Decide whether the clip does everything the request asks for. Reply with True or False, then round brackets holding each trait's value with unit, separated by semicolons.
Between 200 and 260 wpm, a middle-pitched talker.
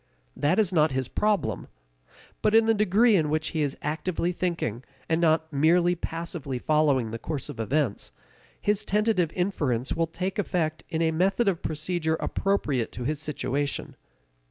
False (160 wpm; 160 Hz)